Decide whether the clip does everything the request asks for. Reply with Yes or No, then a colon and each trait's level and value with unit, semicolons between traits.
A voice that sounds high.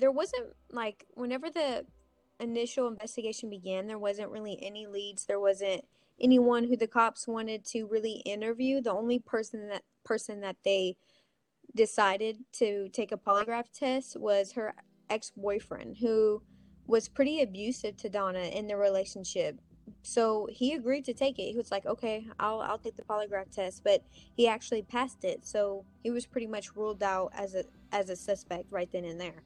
Yes: high, 220 Hz